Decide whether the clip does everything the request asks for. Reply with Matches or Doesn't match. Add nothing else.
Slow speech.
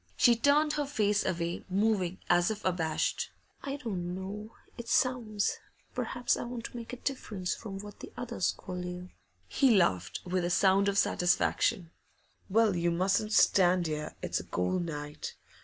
Doesn't match